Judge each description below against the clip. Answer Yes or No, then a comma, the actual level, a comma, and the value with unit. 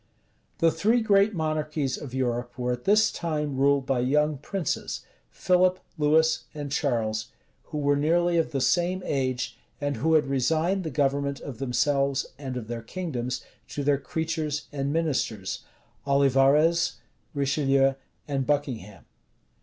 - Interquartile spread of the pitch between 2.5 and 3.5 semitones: Yes, average, 3.2 semitones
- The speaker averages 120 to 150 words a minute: Yes, average, 140 wpm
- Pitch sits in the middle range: Yes, medium, 145 Hz